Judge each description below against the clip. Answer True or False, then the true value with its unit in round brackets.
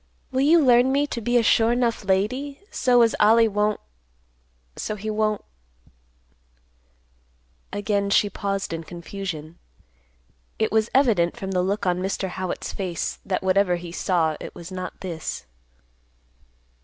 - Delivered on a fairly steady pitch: False (4.3 semitones)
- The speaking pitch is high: True (200 Hz)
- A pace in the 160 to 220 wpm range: False (140 wpm)